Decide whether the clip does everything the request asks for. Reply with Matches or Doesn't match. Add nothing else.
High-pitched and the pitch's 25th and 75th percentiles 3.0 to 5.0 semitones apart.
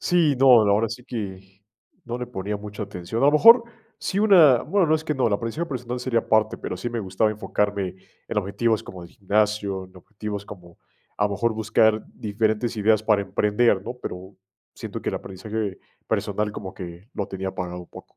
Doesn't match